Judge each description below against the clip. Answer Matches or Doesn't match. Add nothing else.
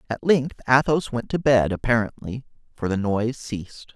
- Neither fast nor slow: Matches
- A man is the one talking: Matches